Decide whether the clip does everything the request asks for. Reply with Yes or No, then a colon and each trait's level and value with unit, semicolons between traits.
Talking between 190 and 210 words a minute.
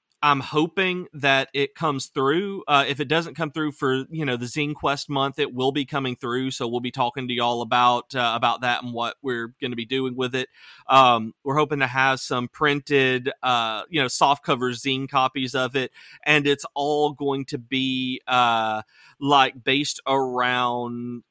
Yes: average, 195 wpm